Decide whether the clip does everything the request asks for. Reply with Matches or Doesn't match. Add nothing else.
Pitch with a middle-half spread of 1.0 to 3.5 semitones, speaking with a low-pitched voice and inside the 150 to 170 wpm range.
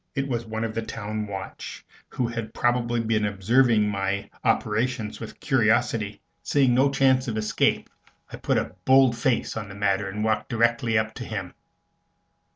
Matches